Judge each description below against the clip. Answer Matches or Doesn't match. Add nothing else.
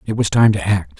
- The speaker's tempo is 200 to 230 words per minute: Doesn't match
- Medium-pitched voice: Doesn't match